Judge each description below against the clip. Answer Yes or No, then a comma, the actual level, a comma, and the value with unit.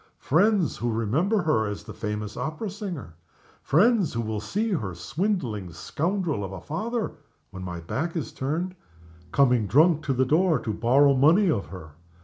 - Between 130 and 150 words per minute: No, average, 165 wpm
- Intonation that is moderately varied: No, wide, 9.0 semitones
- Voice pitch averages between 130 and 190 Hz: Yes, medium, 140 Hz